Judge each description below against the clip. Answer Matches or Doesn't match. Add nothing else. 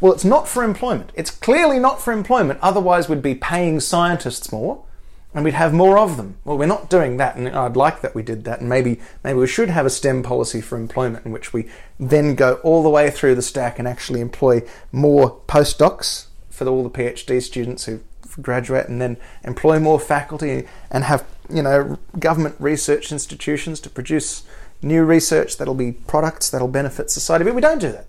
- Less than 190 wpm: Doesn't match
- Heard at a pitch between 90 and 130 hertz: Doesn't match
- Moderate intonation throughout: Matches